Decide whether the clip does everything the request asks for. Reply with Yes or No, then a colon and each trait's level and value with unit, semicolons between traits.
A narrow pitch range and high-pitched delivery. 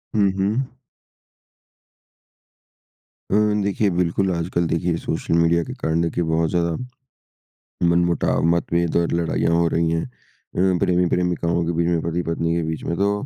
No: narrow, 1.2 semitones; very low, 85 Hz